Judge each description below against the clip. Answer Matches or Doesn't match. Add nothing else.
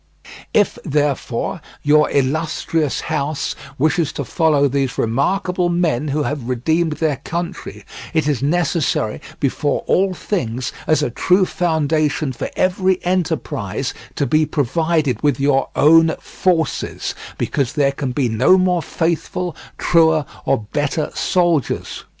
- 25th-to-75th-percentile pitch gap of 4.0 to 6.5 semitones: Doesn't match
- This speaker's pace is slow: Matches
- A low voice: Doesn't match